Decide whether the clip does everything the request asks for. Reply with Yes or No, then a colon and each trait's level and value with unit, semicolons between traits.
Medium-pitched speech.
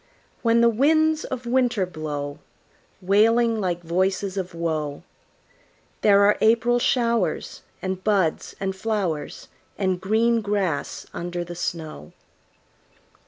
No: high, 195 Hz